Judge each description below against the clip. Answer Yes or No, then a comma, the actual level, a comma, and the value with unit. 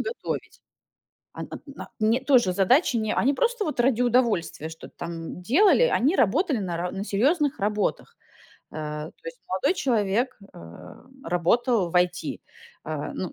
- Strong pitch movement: Yes, wide, 7.5 semitones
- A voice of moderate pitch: No, high, 230 Hz